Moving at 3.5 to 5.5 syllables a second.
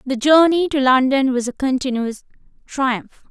Yes: 4.5 syllables/s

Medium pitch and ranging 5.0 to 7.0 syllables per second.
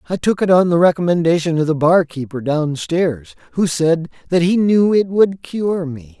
No: medium, 165 Hz; 4.6 syllables/s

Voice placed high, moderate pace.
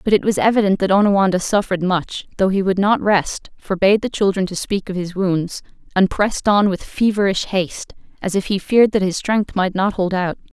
No: high, 195 Hz; fast, 215 wpm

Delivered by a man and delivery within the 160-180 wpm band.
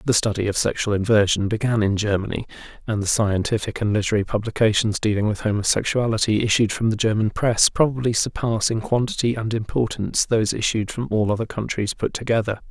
Yes: male; average, 170 wpm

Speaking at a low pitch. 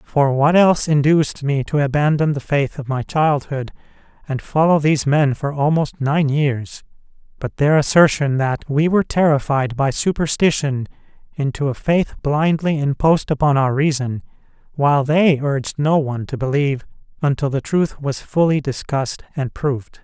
No: medium, 145 Hz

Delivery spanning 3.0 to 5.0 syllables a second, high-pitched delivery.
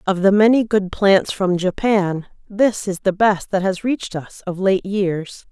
Yes: 4.1 syllables/s; high, 195 Hz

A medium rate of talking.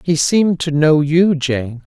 Yes: average, 185 wpm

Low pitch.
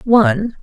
No: high, 230 Hz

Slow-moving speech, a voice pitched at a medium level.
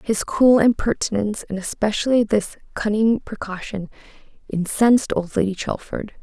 No: slow, 115 wpm; high, 210 Hz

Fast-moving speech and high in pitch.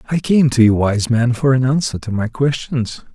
No: fast, 230 wpm; low, 125 Hz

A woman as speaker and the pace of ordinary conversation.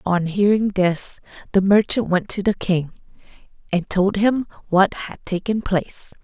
Yes: female; average, 155 wpm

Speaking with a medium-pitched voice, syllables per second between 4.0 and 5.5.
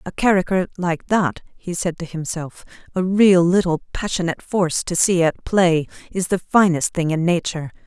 Yes: medium, 175 Hz; 5.1 syllables/s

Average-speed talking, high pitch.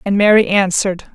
Yes: average, 155 wpm; high, 195 Hz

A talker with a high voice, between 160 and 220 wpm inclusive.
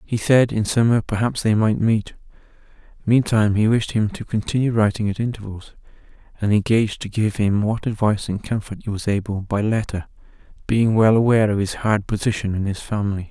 No: low, 105 Hz; average, 185 wpm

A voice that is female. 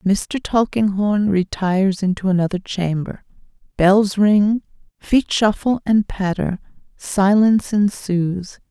Yes: female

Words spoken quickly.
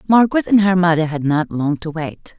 Yes: fast, 225 wpm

